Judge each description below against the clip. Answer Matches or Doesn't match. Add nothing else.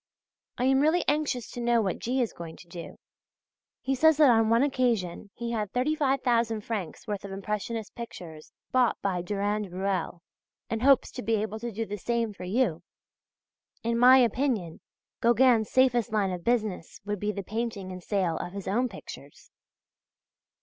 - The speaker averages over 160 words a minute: Matches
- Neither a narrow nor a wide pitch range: Matches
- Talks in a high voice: Matches